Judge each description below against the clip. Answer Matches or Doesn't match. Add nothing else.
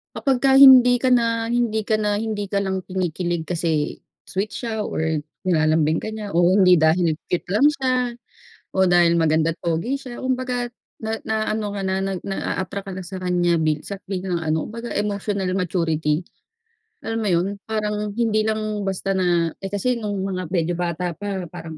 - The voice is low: Doesn't match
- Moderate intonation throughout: Matches